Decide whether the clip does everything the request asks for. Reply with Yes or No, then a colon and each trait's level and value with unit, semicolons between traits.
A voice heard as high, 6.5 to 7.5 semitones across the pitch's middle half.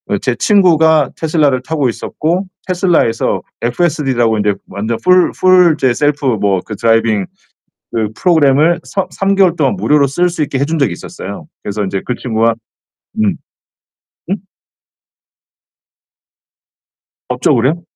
No: medium, 140 Hz; wide, 6.8 semitones